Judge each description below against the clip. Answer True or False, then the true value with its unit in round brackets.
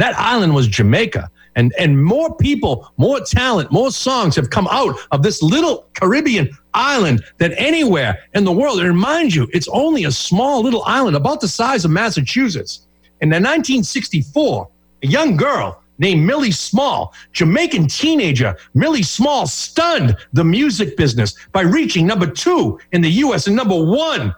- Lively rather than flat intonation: True (8.6 semitones)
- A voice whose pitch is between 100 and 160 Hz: False (175 Hz)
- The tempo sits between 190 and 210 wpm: False (160 wpm)